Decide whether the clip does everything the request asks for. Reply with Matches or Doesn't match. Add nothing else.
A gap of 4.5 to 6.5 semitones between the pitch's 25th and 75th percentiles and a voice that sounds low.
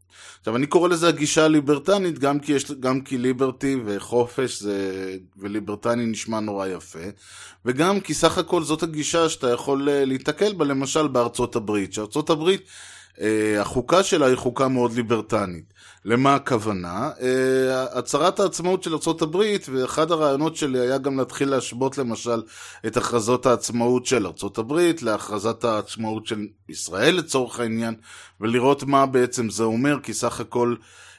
Matches